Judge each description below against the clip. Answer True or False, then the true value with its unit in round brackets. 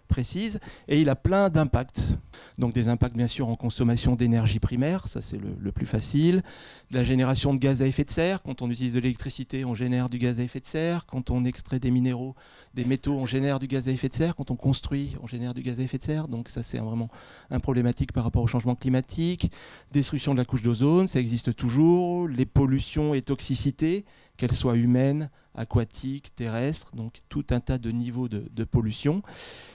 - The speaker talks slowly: False (210 wpm)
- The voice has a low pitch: True (130 Hz)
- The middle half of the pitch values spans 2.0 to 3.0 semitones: True (2.5 semitones)